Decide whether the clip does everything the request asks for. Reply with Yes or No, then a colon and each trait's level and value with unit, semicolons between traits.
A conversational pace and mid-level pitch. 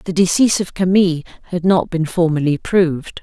Yes: average, 165 wpm; medium, 175 Hz